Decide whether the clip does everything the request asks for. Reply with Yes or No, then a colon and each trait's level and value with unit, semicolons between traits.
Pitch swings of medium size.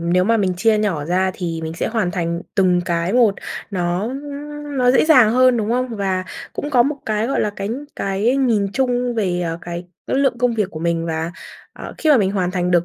No: wide, 5.8 semitones